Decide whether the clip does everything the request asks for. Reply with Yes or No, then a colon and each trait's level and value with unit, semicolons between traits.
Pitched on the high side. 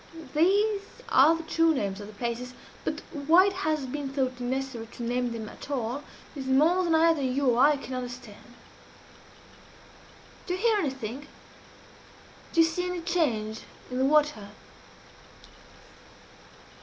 Yes: very high, 275 Hz